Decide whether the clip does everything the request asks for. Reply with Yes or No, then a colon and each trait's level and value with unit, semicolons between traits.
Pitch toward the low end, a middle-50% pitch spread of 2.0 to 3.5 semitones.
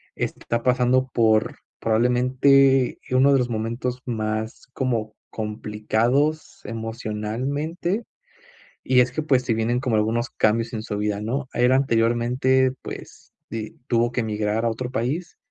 Yes: low, 120 Hz; average, 2.8 semitones